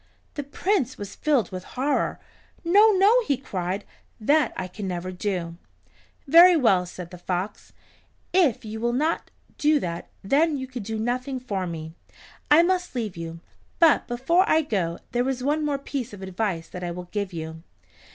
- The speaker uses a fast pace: No, average, 175 wpm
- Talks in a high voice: Yes, high, 235 Hz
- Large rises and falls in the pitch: Yes, wide, 8.3 semitones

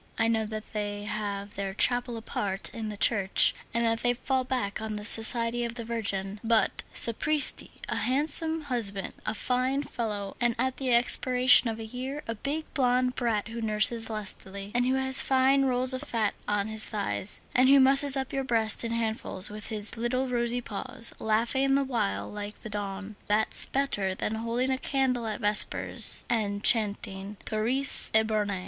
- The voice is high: Yes, high, 230 Hz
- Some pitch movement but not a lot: Yes, average, 3.4 semitones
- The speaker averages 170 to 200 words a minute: Yes, average, 175 wpm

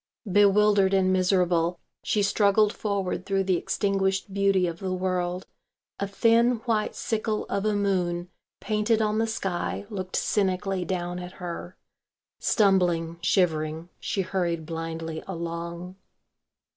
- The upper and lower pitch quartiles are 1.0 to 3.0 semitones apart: Yes, narrow, 2.5 semitones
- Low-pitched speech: No, high, 190 Hz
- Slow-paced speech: Yes, slow, 125 wpm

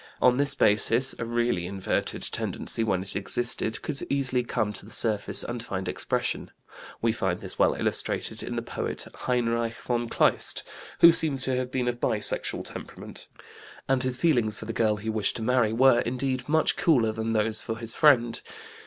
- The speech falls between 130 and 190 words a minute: Yes, average, 180 wpm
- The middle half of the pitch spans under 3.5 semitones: Yes, average, 2.8 semitones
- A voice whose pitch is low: Yes, low, 120 Hz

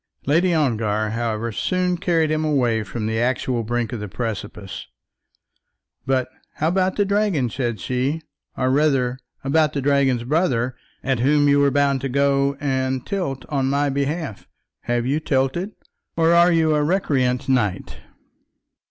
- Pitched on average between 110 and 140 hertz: Yes, low, 135 Hz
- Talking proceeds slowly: No, average, 150 wpm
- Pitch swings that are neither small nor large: Yes, average, 4.2 semitones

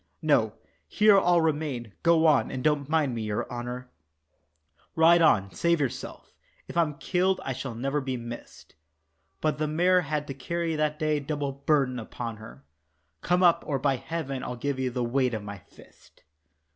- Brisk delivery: No, average, 175 wpm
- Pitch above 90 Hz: Yes, medium, 140 Hz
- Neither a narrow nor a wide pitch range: Yes, average, 4.5 semitones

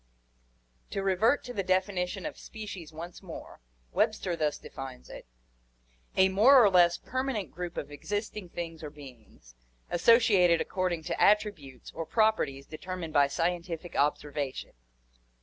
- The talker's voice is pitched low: No, medium, 175 Hz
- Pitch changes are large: No, average, 4.8 semitones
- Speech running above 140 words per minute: No, slow, 135 wpm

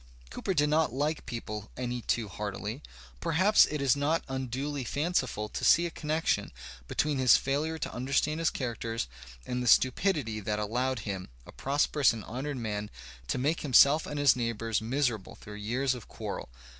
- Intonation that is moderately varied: Yes, average, 4.6 semitones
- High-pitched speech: No, low, 130 Hz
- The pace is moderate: Yes, average, 170 wpm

